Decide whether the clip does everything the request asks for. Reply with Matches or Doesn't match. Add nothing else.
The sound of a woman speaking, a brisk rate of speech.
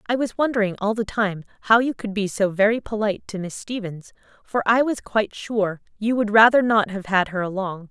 Matches